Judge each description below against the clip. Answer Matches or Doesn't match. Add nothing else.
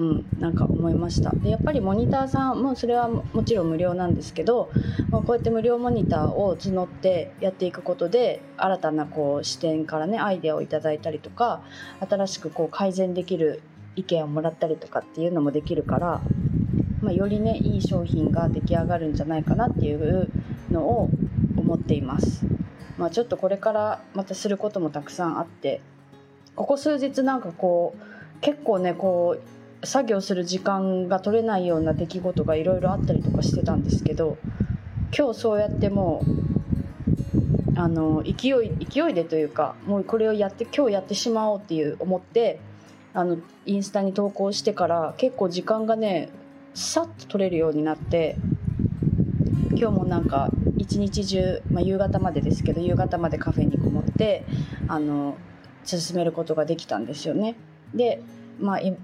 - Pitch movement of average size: Matches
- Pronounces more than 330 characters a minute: Matches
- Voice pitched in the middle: Matches